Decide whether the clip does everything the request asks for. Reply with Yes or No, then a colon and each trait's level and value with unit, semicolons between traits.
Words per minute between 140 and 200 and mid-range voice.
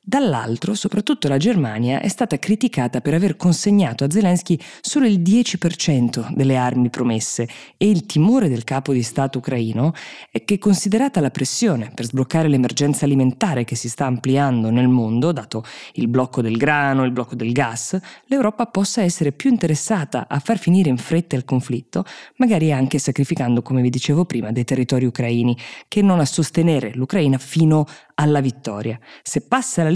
Yes: average, 165 wpm; medium, 145 Hz